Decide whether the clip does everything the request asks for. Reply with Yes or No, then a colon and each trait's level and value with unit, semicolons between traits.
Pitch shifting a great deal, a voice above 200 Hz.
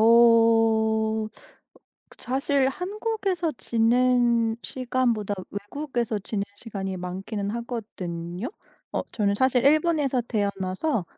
No: average, 3.9 semitones; high, 230 Hz